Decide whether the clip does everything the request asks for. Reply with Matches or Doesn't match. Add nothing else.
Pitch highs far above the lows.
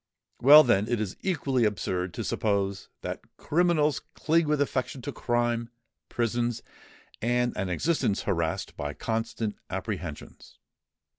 Matches